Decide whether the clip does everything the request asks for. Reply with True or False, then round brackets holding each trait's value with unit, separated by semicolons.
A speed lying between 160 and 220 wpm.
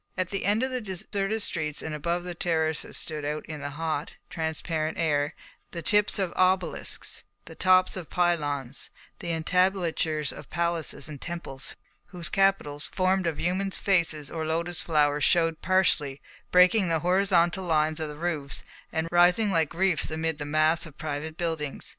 True (165 wpm)